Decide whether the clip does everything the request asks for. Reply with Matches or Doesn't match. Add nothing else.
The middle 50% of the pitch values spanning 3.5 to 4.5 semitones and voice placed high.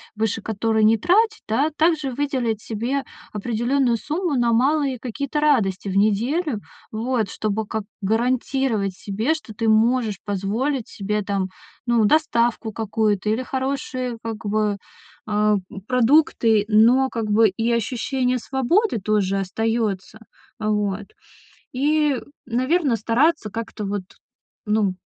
Matches